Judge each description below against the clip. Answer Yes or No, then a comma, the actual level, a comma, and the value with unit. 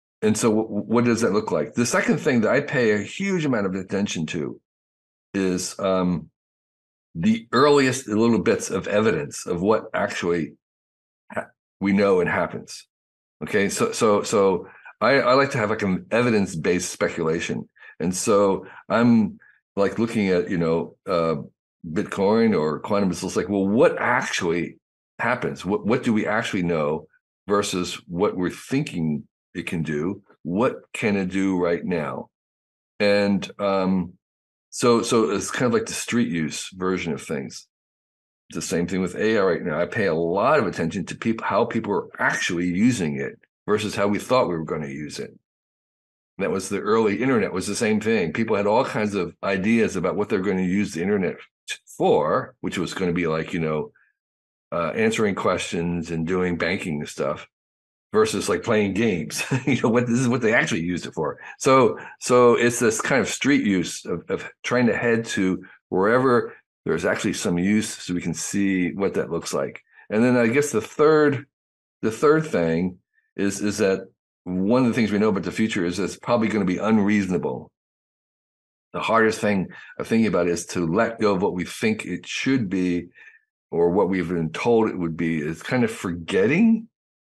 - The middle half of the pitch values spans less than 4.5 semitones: No, average, 5.1 semitones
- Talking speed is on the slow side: No, average, 185 wpm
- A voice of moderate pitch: No, very low, 95 Hz